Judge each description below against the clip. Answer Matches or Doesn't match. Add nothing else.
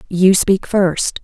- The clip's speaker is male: Doesn't match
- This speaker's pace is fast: Doesn't match